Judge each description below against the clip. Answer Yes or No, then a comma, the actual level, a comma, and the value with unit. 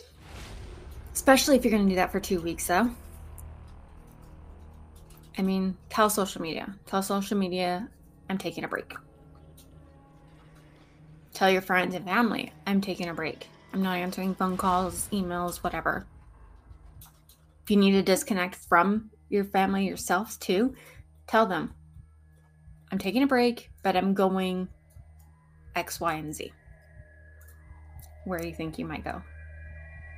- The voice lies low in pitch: No, medium, 175 Hz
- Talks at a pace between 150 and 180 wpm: No, slow, 135 wpm